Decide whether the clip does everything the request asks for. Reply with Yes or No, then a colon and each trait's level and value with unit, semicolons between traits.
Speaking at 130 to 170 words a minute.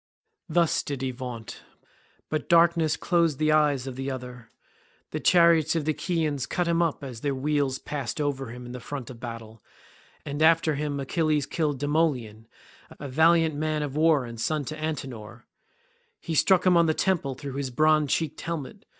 No: average, 185 wpm